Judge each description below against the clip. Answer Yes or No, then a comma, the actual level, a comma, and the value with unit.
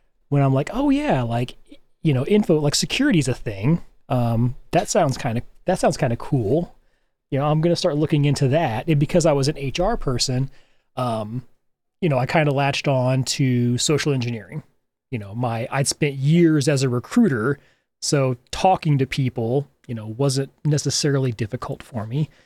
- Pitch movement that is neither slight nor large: Yes, average, 3.8 semitones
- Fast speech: No, average, 185 wpm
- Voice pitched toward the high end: No, medium, 140 Hz